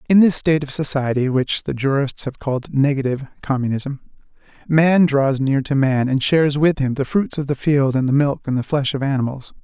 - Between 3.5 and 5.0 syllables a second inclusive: No, 5.4 syllables/s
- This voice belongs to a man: Yes, male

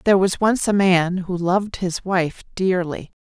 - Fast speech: No, average, 185 wpm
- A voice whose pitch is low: No, medium, 185 Hz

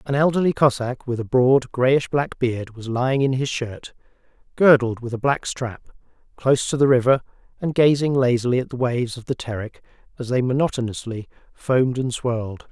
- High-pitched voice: No, low, 125 Hz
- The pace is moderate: Yes, average, 180 wpm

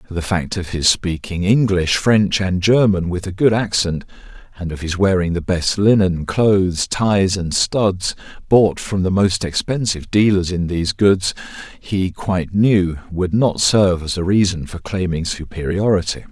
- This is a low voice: Yes, very low, 95 Hz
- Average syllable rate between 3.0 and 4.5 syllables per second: Yes, 4.4 syllables/s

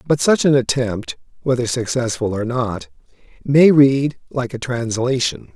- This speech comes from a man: Yes, male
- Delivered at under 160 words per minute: Yes, average, 140 wpm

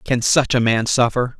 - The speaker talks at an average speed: No, fast, 215 wpm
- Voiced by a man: Yes, male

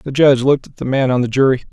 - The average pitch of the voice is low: Yes, low, 130 Hz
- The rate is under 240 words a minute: No, fast, 315 wpm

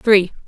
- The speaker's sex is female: Yes, female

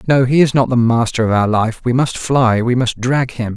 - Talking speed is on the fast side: Yes, fast, 270 wpm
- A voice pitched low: Yes, low, 120 Hz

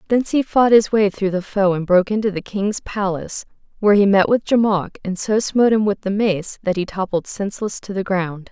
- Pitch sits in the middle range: No, high, 200 Hz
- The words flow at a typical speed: No, fast, 235 wpm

